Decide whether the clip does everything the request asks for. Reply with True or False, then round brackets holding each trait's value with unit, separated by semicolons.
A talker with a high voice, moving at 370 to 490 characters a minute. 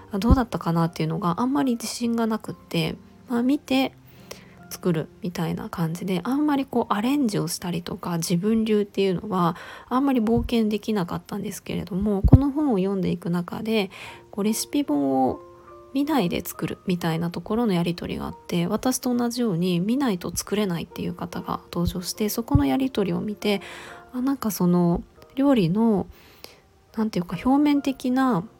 True (210 Hz; 375 characters per minute)